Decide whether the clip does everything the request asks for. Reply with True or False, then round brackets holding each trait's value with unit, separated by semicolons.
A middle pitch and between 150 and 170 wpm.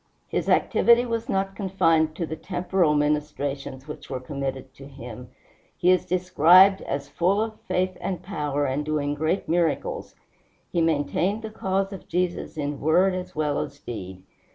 True (160 Hz; 160 wpm)